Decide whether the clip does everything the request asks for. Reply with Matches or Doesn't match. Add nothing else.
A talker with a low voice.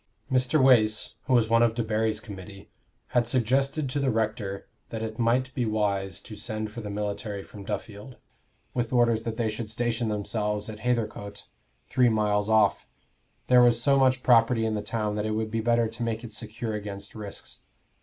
Matches